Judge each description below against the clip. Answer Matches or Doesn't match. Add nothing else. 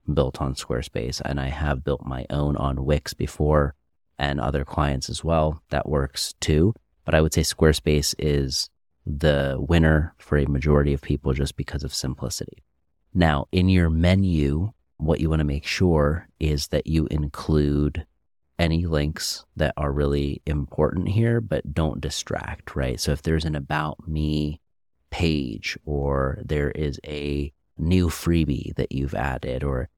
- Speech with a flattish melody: Matches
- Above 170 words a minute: Doesn't match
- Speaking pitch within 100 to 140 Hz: Doesn't match